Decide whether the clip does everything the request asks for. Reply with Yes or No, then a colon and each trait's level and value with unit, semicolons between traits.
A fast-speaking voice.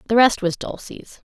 No: average, 185 wpm